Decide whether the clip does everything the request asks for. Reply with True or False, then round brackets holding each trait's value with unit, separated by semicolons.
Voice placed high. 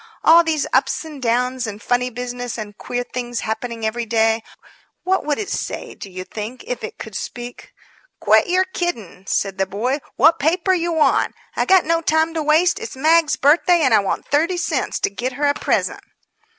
True (260 Hz)